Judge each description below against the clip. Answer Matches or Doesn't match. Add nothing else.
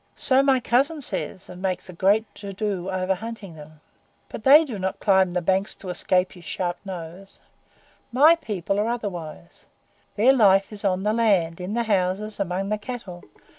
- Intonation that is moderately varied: Matches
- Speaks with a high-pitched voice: Matches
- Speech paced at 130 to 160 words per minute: Doesn't match